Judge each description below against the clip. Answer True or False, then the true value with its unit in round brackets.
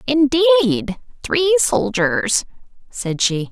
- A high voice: True (255 Hz)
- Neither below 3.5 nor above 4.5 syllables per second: True (3.6 syllables/s)